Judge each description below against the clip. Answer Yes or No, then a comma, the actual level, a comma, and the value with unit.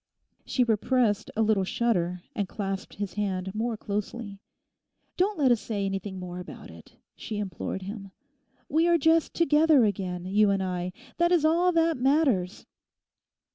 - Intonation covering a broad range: Yes, wide, 6.4 semitones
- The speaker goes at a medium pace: Yes, average, 160 wpm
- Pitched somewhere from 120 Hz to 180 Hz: No, high, 210 Hz